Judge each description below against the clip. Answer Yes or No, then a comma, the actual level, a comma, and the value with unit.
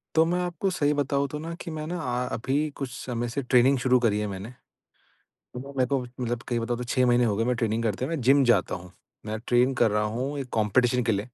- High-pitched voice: No, low, 125 Hz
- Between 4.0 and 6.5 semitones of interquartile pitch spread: No, average, 3.1 semitones